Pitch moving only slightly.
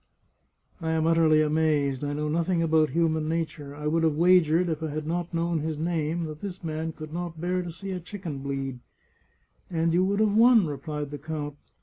Yes: narrow, 2.2 semitones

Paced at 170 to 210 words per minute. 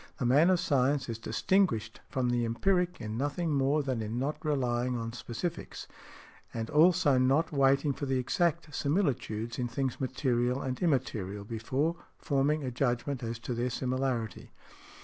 No: average, 155 wpm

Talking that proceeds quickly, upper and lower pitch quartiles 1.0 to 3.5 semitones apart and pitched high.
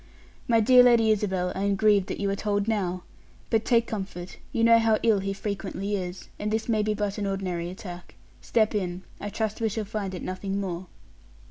Yes: fast, 210 wpm; narrow, 2.5 semitones; high, 205 Hz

